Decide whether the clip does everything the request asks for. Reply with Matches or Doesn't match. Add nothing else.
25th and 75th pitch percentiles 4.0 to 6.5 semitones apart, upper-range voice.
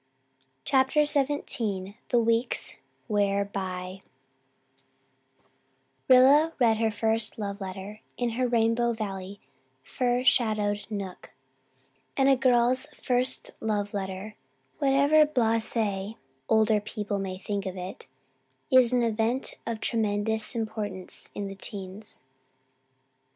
Doesn't match